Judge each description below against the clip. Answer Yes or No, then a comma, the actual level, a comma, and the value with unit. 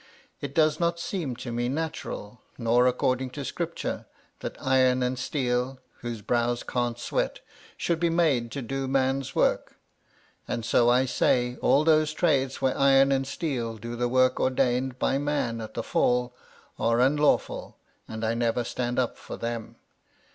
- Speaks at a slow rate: No, average, 160 wpm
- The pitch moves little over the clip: Yes, narrow, 2.2 semitones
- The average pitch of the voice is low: Yes, low, 130 Hz